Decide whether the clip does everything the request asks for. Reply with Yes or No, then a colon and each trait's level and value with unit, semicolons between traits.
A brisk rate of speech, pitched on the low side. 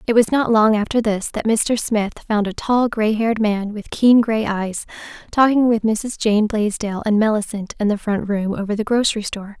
No: fast, 215 wpm; high, 215 Hz